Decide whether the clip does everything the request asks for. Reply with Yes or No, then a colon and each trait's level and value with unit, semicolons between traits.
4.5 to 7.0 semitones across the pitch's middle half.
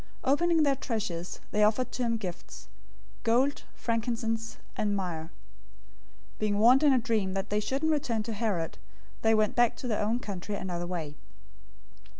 No: average, 3.6 semitones